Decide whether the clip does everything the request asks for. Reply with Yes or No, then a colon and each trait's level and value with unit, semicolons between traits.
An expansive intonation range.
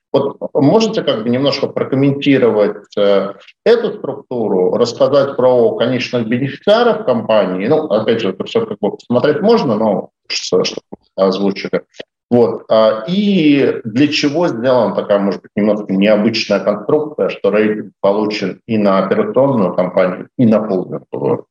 Yes: wide, 6.1 semitones